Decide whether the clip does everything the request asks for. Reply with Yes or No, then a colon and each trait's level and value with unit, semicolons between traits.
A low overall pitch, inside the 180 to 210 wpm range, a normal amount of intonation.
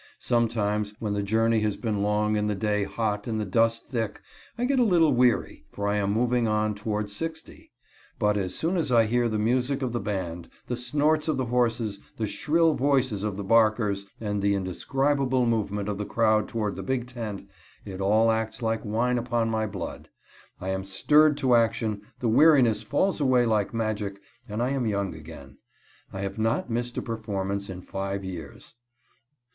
Yes: low, 110 Hz; average, 190 wpm; average, 3.2 semitones